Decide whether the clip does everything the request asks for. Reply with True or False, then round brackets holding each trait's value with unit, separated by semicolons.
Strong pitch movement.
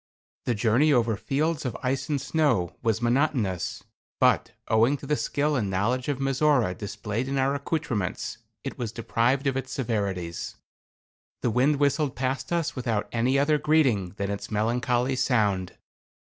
False (4.7 semitones)